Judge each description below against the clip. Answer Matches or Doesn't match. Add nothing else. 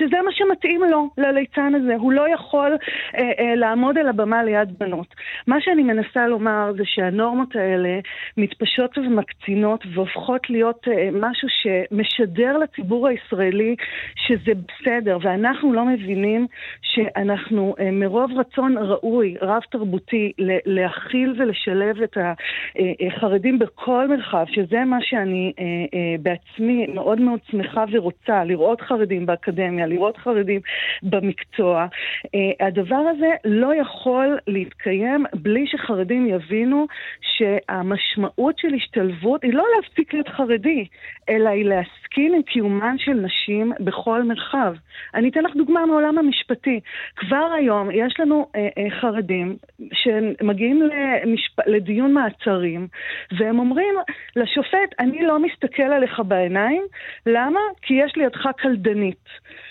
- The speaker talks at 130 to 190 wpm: Doesn't match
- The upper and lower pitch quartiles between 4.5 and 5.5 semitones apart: Matches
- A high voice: Matches